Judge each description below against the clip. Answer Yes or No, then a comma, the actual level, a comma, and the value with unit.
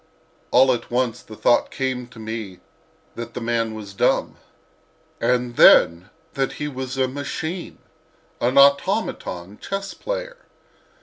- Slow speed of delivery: Yes, slow, 125 wpm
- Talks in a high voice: No, low, 125 Hz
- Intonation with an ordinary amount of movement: Yes, average, 3.7 semitones